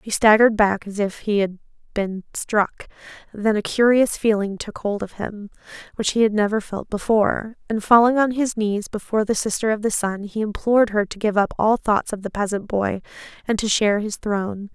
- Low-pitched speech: No, high, 210 Hz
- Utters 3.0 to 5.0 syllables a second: No, 5.3 syllables/s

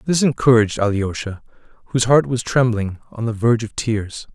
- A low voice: Yes, low, 115 Hz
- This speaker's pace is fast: No, average, 165 wpm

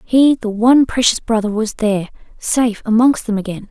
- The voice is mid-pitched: No, high, 225 Hz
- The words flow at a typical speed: Yes, average, 180 wpm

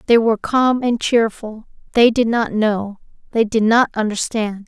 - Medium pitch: No, high, 225 Hz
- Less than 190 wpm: Yes, average, 165 wpm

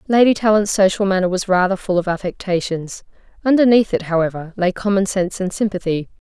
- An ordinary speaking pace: Yes, average, 155 wpm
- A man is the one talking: No, female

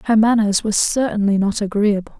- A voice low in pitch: No, high, 210 Hz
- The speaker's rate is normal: Yes, average, 165 wpm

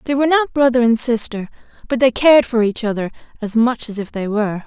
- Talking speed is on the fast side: Yes, fast, 230 wpm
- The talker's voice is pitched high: Yes, high, 235 Hz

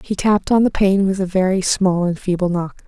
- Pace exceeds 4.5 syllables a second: Yes, 5.5 syllables/s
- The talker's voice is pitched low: No, high, 190 Hz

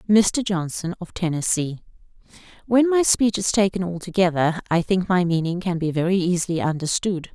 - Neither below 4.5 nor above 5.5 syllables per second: Yes, 5.2 syllables/s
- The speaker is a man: No, female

